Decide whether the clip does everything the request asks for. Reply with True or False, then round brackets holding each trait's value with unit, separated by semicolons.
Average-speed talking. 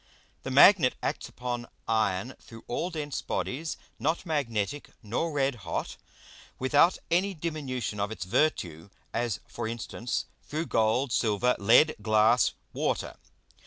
False (125 wpm)